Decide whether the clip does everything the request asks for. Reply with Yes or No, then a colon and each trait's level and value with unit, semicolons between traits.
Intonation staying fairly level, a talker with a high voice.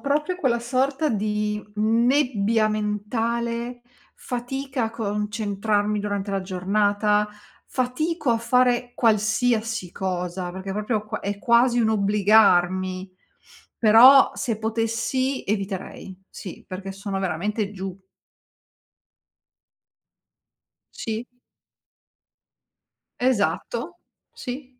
No: average, 3.2 semitones; high, 215 Hz